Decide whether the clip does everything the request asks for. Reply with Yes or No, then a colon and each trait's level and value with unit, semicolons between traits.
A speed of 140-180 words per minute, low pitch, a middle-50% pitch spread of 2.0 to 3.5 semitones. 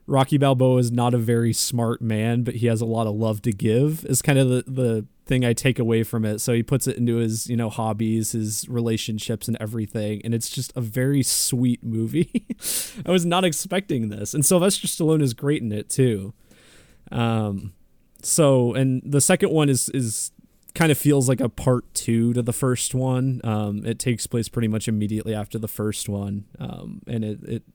No: fast, 205 wpm; low, 120 Hz; average, 3.0 semitones